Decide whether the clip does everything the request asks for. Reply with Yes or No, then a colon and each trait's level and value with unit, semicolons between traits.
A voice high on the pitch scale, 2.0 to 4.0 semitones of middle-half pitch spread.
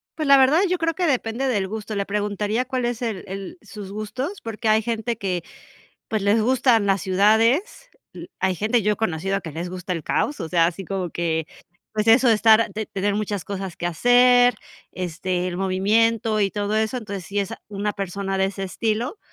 Yes: high, 210 Hz; average, 3.2 semitones